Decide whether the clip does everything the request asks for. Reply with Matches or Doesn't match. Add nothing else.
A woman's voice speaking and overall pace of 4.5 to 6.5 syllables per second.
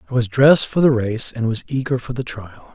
Doesn't match